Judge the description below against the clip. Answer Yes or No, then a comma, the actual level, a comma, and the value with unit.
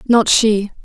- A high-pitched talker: Yes, high, 215 Hz